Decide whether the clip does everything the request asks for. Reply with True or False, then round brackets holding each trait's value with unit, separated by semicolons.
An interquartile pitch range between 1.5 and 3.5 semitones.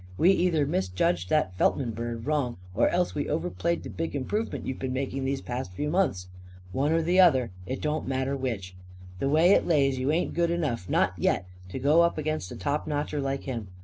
False (4.1 semitones)